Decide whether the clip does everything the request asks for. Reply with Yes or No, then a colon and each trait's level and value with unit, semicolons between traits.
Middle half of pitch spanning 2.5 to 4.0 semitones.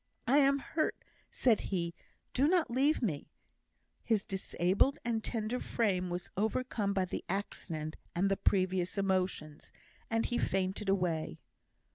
No: average, 4.6 semitones